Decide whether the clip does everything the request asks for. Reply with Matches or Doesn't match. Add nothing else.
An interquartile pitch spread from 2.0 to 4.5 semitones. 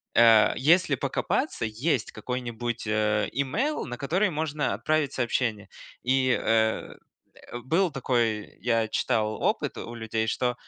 Matches